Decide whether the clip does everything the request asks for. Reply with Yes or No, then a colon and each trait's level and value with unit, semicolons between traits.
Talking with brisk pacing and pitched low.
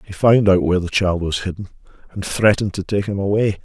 Yes: fast, 230 wpm; very low, 95 Hz